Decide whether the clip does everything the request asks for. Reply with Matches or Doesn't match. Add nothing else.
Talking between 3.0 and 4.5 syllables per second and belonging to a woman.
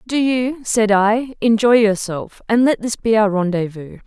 Matches